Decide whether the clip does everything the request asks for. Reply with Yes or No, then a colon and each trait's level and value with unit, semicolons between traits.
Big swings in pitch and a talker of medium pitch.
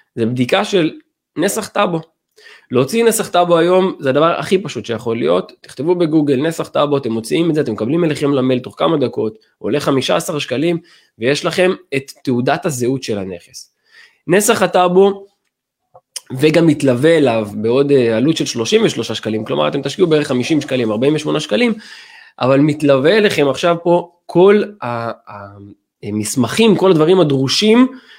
Yes: wide, 6.4 semitones; medium, 155 Hz